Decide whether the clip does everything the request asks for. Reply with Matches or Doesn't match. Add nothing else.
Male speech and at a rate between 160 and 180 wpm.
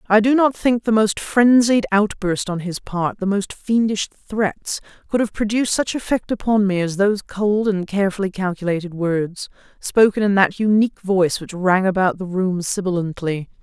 Doesn't match